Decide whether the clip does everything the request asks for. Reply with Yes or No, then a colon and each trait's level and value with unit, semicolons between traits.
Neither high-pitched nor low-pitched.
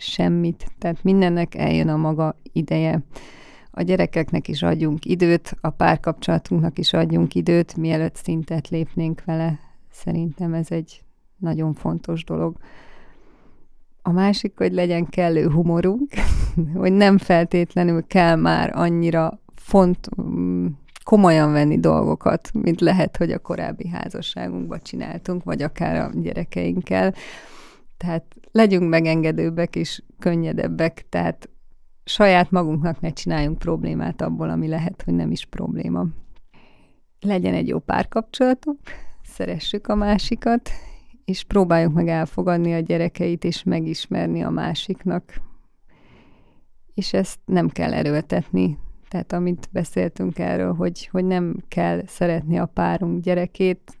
Yes: medium, 165 Hz